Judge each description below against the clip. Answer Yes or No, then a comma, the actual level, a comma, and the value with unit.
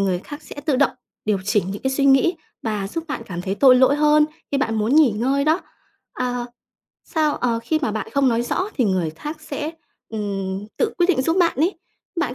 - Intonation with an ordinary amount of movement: No, wide, 6.2 semitones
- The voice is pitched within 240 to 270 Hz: Yes, very high, 260 Hz